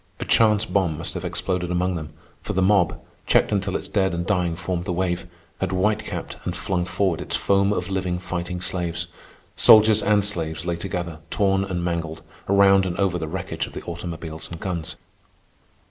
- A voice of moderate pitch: No, very low, 90 Hz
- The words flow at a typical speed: Yes, average, 190 wpm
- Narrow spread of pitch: Yes, narrow, 2.2 semitones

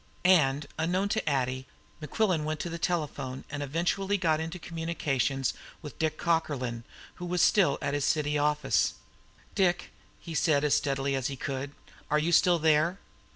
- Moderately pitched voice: Yes, medium, 155 Hz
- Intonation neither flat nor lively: Yes, average, 3.6 semitones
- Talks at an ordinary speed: Yes, average, 160 wpm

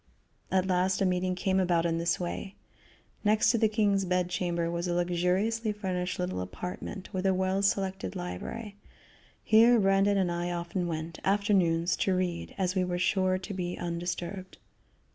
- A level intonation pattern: Yes, narrow, 1.9 semitones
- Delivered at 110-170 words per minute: Yes, average, 165 wpm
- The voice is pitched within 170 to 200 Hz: Yes, medium, 185 Hz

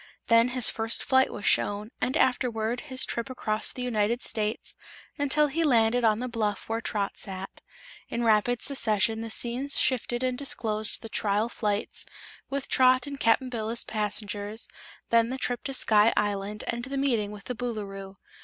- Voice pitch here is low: No, high, 230 Hz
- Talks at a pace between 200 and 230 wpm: No, average, 175 wpm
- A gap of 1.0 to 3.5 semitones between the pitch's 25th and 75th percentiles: Yes, average, 3.1 semitones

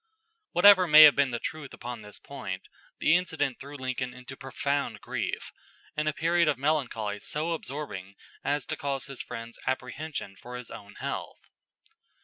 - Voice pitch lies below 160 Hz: Yes, medium, 140 Hz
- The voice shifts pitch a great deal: No, average, 3.8 semitones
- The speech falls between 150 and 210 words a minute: Yes, average, 160 wpm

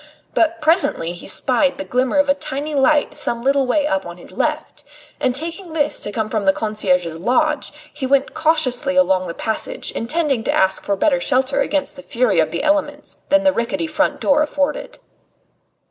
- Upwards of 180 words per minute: Yes, average, 190 wpm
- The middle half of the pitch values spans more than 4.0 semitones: Yes, average, 5.2 semitones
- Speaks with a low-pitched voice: No, very high, 275 Hz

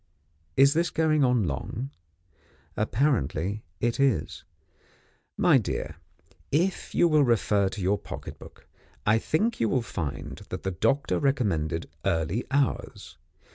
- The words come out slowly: Yes, slow, 130 wpm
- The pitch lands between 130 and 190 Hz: No, low, 115 Hz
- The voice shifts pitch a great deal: Yes, wide, 7.8 semitones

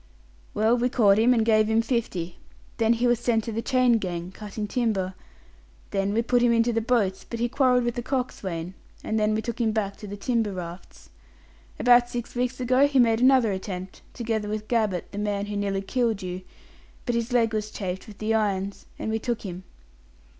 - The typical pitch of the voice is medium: No, high, 220 Hz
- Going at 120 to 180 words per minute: No, fast, 205 wpm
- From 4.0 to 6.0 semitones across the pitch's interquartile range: No, average, 3.1 semitones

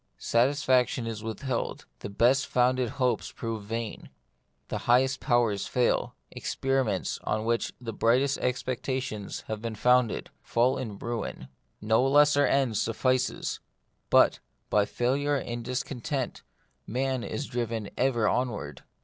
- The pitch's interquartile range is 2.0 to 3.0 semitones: Yes, narrow, 2.5 semitones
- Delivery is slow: Yes, slow, 130 wpm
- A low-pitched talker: Yes, low, 120 Hz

